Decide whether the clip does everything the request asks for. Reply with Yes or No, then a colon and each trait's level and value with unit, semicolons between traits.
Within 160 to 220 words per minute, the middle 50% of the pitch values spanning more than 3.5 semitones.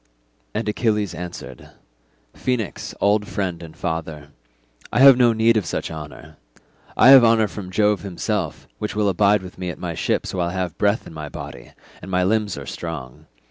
Yes: average, 180 wpm; average, 4.0 semitones